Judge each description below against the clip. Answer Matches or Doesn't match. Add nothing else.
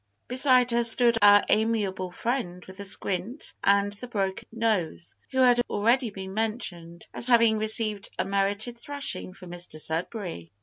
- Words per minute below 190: Matches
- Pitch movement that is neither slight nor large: Matches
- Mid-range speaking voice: Doesn't match